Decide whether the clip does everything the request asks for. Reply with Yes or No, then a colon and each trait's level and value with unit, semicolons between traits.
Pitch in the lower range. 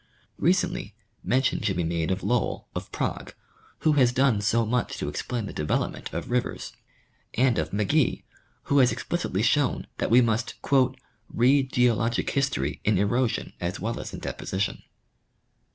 Yes: low, 115 Hz